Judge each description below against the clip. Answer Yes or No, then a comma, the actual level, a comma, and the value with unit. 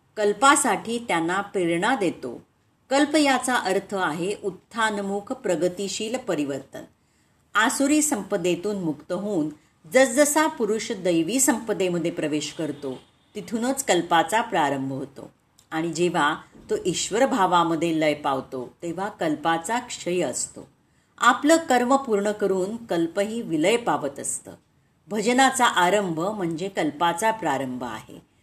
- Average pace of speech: Yes, average, 105 wpm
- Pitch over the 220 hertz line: No, high, 200 Hz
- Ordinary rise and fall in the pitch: No, wide, 6.1 semitones